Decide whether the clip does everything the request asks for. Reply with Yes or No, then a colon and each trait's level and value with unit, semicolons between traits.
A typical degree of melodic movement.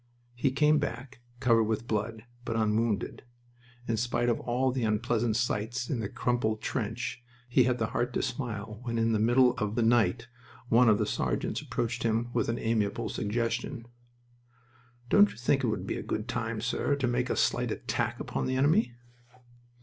No: narrow, 2.0 semitones